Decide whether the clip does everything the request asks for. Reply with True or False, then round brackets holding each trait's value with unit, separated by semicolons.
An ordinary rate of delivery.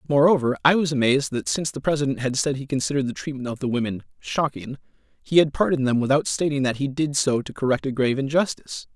False (220 wpm)